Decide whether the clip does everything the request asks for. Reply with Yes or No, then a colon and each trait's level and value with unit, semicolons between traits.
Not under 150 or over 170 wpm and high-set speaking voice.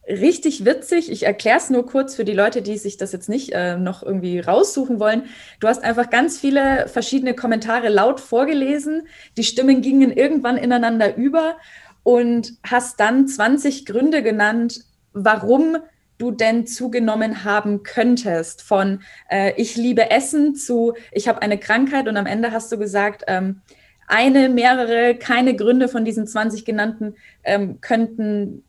Yes: average, 155 wpm; high, 235 Hz